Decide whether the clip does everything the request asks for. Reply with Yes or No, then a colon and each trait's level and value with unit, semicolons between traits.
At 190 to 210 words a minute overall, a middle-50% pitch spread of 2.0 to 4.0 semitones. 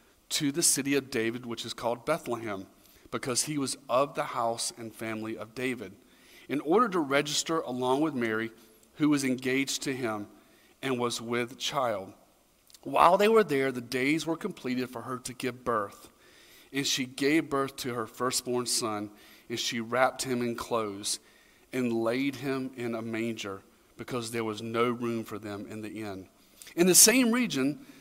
No: average, 175 wpm; average, 3.2 semitones